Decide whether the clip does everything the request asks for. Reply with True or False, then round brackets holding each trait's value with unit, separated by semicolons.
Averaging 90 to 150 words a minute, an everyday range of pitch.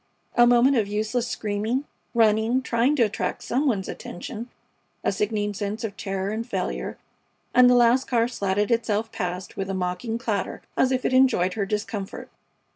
False (170 wpm; 3.2 semitones)